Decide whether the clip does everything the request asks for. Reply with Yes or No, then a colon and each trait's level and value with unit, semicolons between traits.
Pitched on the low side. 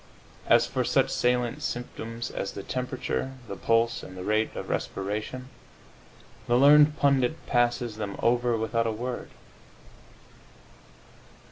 Yes: low, 120 Hz